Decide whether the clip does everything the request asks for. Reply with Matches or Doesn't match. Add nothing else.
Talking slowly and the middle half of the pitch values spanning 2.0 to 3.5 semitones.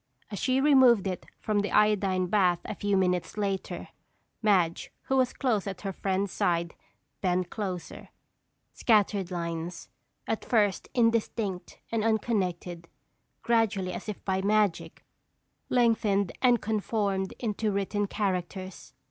Matches